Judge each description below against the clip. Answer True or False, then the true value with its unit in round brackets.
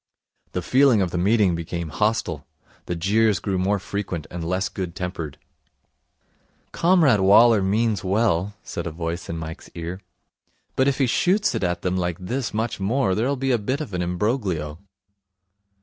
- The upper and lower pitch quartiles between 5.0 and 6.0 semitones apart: False (4.6 semitones)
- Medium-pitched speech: False (95 Hz)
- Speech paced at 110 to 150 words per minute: False (165 wpm)